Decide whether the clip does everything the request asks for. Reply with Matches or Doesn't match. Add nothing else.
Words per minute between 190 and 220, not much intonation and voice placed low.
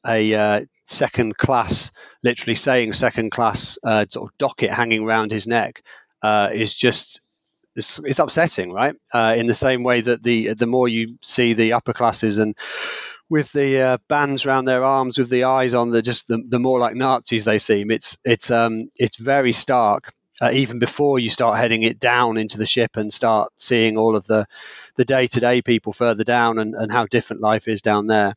Matches